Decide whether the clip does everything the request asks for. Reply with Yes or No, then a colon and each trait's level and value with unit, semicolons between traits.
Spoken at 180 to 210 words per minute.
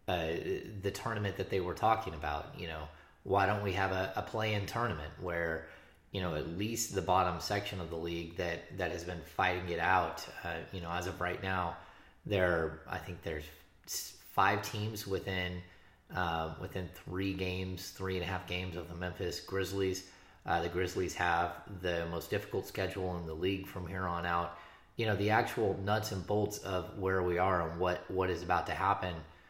Yes: average, 200 wpm